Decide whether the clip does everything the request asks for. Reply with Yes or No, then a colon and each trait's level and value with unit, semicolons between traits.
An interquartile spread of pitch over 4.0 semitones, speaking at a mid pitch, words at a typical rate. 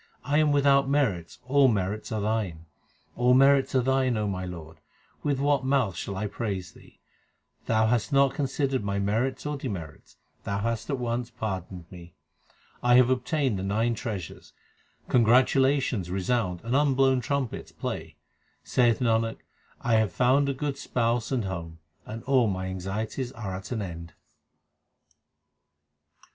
No: average, 5.2 semitones; low, 115 Hz; average, 150 wpm